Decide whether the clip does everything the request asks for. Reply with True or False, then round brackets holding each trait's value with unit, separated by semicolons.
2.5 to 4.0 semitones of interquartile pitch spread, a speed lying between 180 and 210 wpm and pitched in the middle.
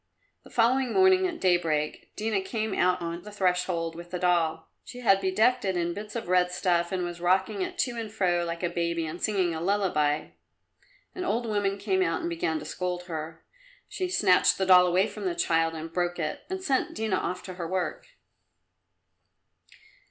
True (3.7 semitones; 195 wpm; 180 Hz)